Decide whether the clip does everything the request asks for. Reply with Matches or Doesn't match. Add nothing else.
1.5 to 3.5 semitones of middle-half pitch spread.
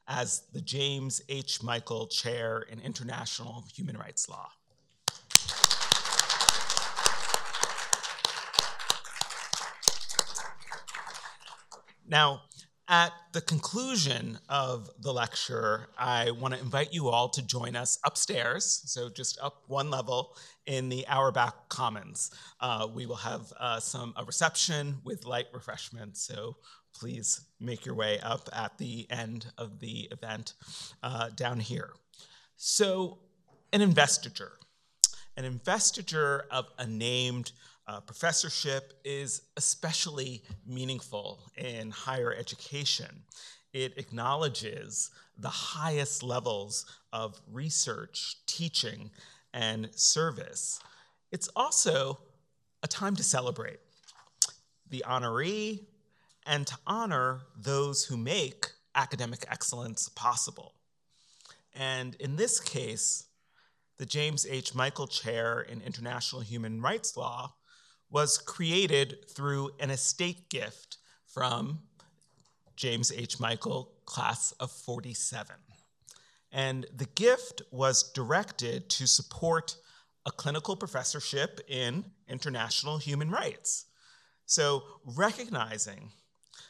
Doesn't match